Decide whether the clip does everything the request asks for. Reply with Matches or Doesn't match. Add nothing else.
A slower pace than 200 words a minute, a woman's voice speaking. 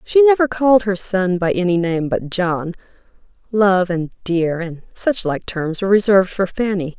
Matches